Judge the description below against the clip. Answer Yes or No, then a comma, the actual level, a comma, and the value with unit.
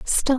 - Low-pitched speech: No, very high, 265 Hz